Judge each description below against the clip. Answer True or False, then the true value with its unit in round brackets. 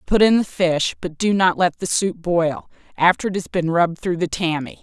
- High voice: False (175 Hz)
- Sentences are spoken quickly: True (235 wpm)